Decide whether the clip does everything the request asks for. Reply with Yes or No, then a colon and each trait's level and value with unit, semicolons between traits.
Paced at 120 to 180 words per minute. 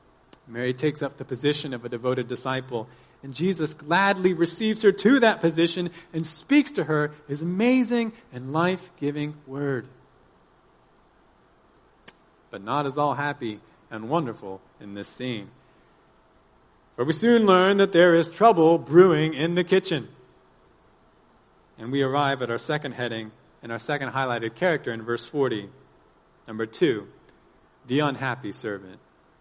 Yes: average, 140 wpm